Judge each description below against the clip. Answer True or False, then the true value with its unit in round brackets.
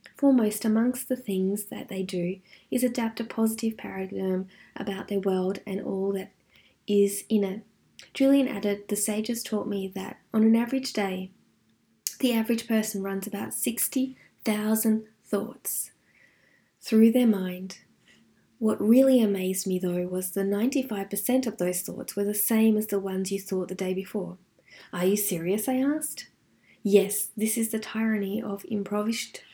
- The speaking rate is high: False (155 wpm)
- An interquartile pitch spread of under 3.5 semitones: True (2.7 semitones)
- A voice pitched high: True (205 Hz)